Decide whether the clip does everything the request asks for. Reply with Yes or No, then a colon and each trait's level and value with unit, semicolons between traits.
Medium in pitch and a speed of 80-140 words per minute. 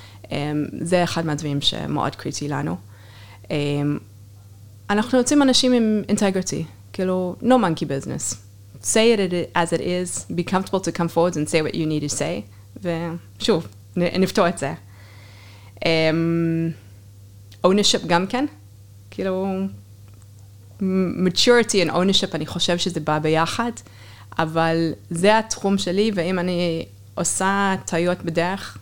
Yes: medium, 165 Hz; average, 125 wpm